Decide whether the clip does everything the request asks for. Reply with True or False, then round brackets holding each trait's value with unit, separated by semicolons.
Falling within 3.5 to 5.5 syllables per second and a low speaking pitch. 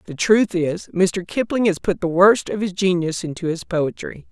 False (4.7 syllables/s; 185 Hz)